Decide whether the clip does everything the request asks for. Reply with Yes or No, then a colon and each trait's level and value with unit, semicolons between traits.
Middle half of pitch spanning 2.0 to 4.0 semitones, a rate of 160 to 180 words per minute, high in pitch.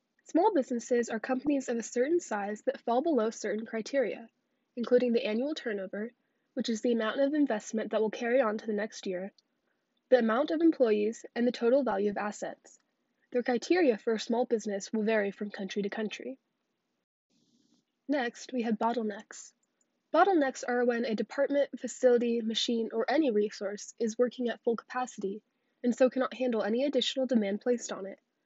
Yes: average, 3.0 semitones; average, 175 wpm; high, 240 Hz